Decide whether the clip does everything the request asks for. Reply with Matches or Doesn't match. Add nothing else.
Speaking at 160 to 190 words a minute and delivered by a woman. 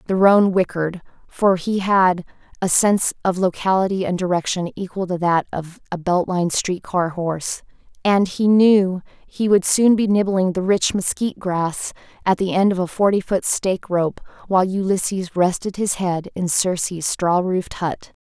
Matches